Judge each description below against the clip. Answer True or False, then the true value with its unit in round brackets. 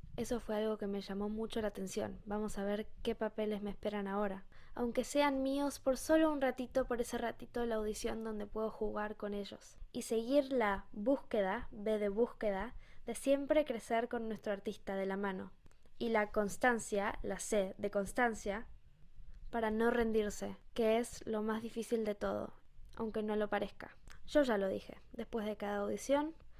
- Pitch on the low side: False (220 Hz)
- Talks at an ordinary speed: True (180 wpm)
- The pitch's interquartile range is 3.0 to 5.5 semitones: False (2.6 semitones)